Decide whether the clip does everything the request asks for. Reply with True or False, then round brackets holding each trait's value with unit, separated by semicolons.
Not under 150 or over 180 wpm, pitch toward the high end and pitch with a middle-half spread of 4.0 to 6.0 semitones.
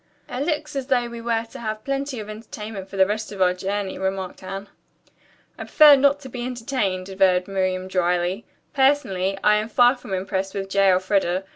False (190 wpm; 205 Hz; 4.4 semitones)